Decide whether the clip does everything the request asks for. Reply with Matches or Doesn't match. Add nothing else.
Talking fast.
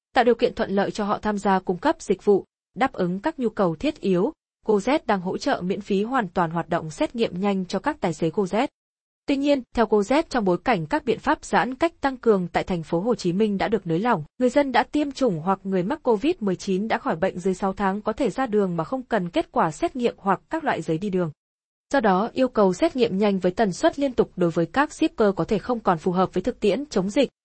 Matches